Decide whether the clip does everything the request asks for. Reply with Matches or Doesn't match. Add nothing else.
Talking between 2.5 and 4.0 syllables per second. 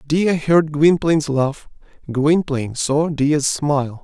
Matches